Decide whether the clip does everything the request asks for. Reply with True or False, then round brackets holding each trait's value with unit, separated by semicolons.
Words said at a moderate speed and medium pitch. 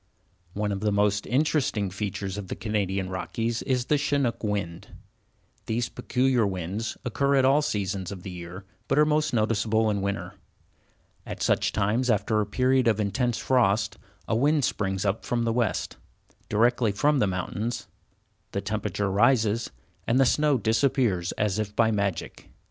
False (160 wpm; 110 Hz)